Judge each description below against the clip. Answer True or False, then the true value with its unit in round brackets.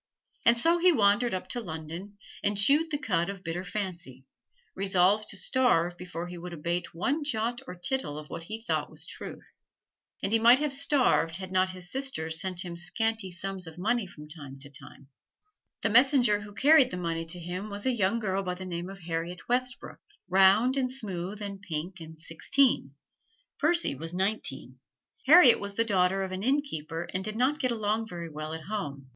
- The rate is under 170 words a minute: False (195 wpm)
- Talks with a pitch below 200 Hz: True (190 Hz)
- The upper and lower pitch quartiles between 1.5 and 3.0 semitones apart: False (5.3 semitones)